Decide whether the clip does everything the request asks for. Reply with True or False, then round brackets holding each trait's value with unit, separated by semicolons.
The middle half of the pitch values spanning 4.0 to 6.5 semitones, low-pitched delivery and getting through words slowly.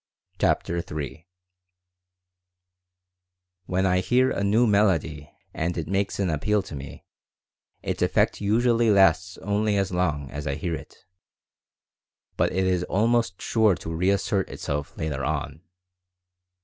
True (4.6 semitones; 90 Hz; 130 wpm)